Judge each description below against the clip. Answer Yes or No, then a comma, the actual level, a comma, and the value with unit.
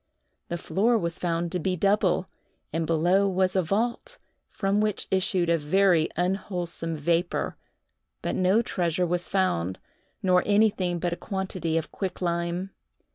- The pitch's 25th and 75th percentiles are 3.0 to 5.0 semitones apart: No, narrow, 2.4 semitones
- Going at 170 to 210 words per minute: No, average, 140 wpm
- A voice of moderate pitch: Yes, medium, 180 Hz